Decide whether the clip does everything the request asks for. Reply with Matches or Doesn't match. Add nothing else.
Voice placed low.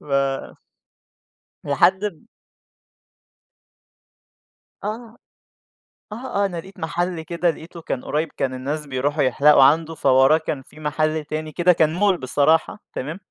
Doesn't match